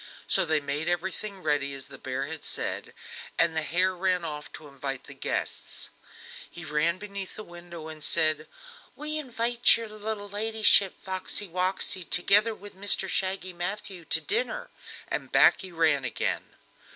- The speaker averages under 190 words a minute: Yes, average, 160 wpm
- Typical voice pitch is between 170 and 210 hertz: Yes, medium, 185 Hz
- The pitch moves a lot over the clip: No, average, 4.4 semitones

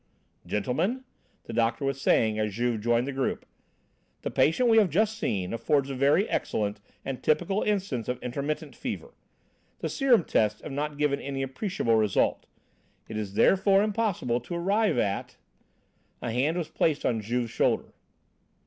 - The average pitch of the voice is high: No, low, 135 Hz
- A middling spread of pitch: No, wide, 8.0 semitones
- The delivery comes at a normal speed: Yes, average, 160 wpm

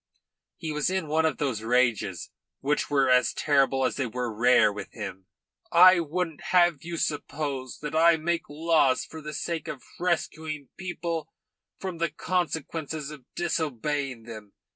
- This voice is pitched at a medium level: Yes, medium, 150 Hz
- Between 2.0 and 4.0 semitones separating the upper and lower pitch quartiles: No, average, 4.5 semitones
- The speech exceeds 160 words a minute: No, average, 155 wpm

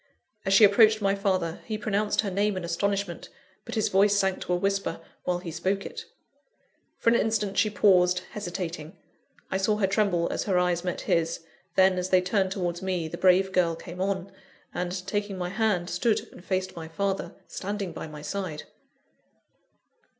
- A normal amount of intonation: No, narrow, 2.2 semitones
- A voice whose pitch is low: No, high, 190 Hz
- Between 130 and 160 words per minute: No, average, 180 wpm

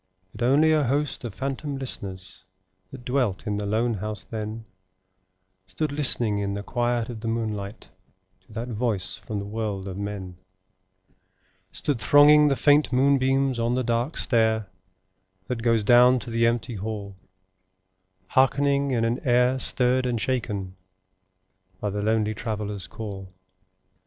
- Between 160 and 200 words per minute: No, average, 145 wpm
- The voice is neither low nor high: No, low, 115 Hz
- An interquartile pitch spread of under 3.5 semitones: No, average, 3.8 semitones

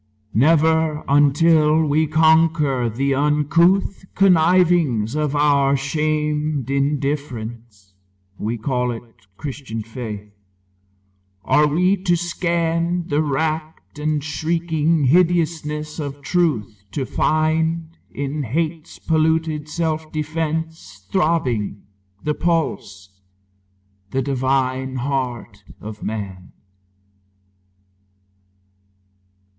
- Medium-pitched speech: Yes, medium, 150 Hz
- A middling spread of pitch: Yes, average, 3.6 semitones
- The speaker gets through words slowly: Yes, slow, 85 wpm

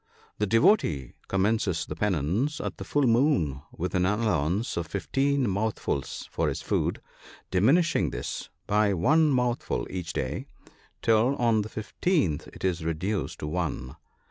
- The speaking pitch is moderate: No, low, 100 Hz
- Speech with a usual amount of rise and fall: No, wide, 6.5 semitones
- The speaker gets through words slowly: No, average, 145 wpm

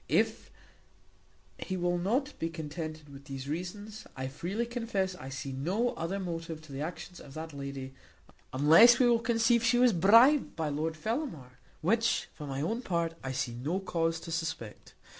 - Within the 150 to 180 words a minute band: Yes, average, 175 wpm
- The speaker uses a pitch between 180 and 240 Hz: No, medium, 165 Hz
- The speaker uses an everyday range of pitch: No, wide, 6.8 semitones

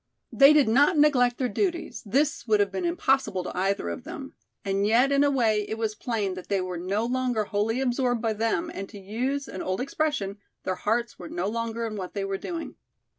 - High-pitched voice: Yes, high, 225 Hz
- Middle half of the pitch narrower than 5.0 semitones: No, average, 5.3 semitones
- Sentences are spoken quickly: Yes, fast, 220 wpm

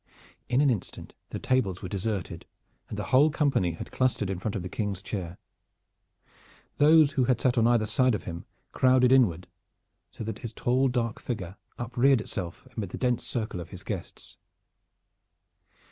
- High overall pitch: No, low, 115 Hz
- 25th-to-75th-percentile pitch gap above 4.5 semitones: Yes, average, 5.1 semitones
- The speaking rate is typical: Yes, average, 170 wpm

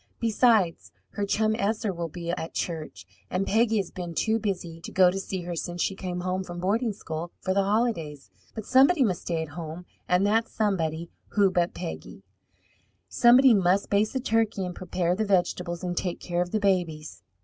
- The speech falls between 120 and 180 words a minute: No, average, 195 wpm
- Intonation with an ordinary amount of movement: Yes, average, 3.6 semitones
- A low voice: No, medium, 185 Hz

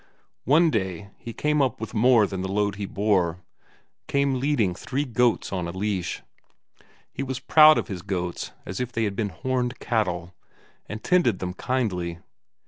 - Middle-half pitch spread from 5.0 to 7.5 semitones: Yes, wide, 5.6 semitones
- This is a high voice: No, low, 110 Hz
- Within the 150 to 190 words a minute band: Yes, average, 170 wpm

